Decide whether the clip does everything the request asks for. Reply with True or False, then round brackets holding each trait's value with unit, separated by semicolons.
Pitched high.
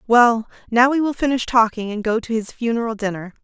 True (230 Hz)